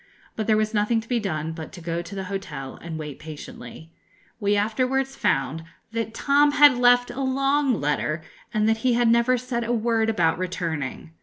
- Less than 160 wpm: No, average, 190 wpm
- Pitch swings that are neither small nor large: No, wide, 6.8 semitones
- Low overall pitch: No, high, 215 Hz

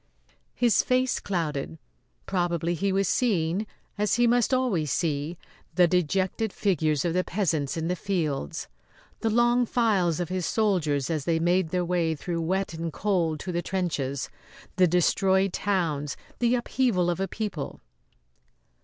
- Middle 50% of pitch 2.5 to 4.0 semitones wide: Yes, average, 3.7 semitones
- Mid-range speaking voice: Yes, medium, 180 Hz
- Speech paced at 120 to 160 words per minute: Yes, average, 150 wpm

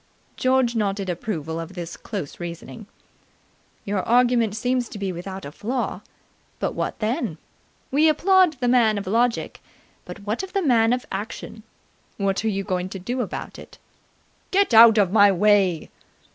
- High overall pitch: Yes, high, 215 Hz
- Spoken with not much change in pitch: No, average, 4.3 semitones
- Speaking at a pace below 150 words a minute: No, average, 160 wpm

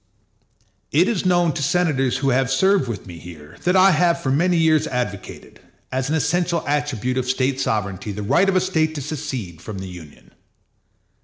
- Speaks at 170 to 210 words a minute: Yes, average, 185 wpm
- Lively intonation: Yes, wide, 7.8 semitones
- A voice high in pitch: No, low, 135 Hz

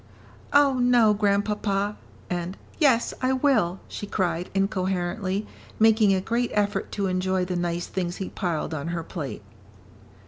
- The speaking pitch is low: No, high, 195 Hz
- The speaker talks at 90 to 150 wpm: Yes, average, 140 wpm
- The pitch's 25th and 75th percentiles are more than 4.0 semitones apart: No, average, 3.4 semitones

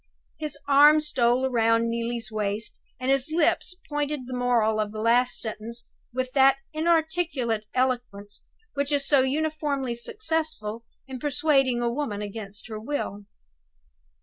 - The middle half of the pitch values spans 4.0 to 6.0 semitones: Yes, average, 4.3 semitones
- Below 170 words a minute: Yes, slow, 135 wpm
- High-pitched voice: Yes, very high, 255 Hz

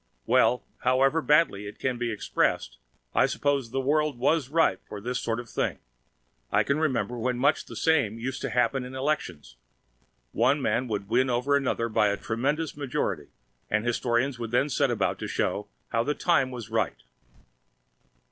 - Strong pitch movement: No, average, 3.6 semitones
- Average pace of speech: Yes, average, 175 wpm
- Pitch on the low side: Yes, low, 125 Hz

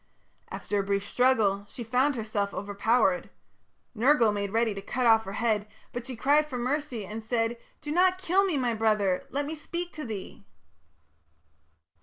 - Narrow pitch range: No, wide, 5.4 semitones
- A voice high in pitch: Yes, high, 230 Hz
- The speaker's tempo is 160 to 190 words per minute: Yes, average, 170 wpm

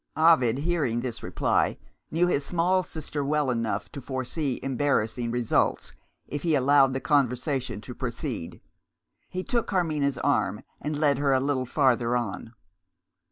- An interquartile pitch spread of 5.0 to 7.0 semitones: No, average, 3.7 semitones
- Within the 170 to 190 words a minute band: No, average, 145 wpm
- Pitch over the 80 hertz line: Yes, medium, 140 Hz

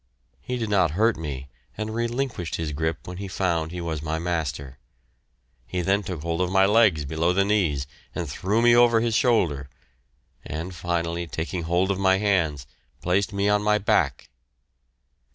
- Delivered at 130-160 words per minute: No, average, 170 wpm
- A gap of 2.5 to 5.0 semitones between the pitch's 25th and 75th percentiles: Yes, average, 4.2 semitones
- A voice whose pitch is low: Yes, very low, 90 Hz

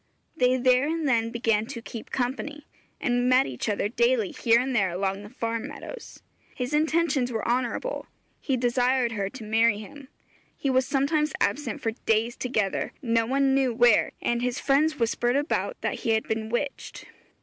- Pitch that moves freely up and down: No, average, 3.3 semitones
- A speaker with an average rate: Yes, average, 175 wpm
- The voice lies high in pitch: Yes, high, 245 Hz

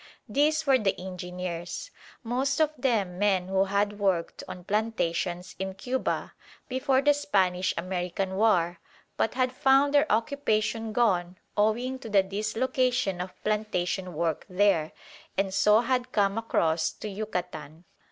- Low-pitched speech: No, high, 205 Hz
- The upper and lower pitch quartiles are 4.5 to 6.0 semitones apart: Yes, average, 5.3 semitones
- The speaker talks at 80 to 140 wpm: Yes, slow, 135 wpm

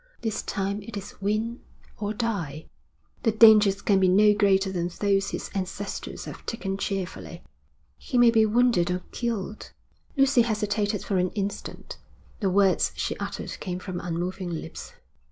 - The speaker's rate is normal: Yes, average, 155 wpm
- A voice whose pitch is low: No, high, 200 Hz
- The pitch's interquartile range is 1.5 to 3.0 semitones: Yes, narrow, 2.6 semitones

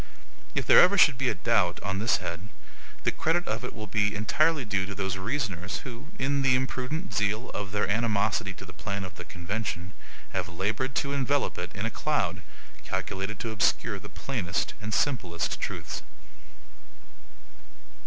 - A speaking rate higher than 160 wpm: Yes, average, 170 wpm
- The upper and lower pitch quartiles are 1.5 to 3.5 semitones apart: No, average, 5.1 semitones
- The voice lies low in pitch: Yes, low, 105 Hz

